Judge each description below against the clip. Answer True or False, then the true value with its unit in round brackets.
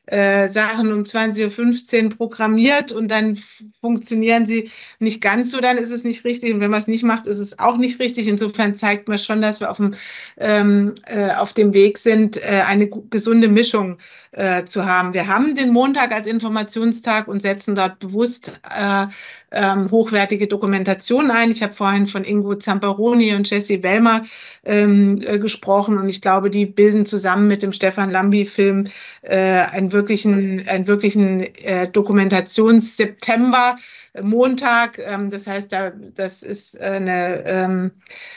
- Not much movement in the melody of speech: True (2.2 semitones)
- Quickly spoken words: False (150 wpm)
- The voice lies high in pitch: True (210 Hz)